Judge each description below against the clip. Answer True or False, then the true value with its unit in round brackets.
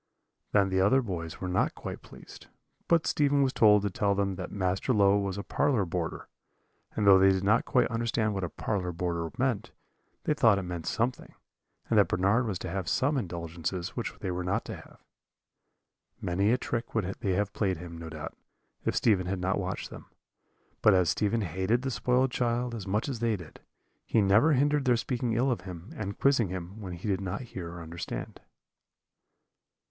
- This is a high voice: False (100 Hz)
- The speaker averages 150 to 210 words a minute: True (200 wpm)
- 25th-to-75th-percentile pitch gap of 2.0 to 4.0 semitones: False (4.4 semitones)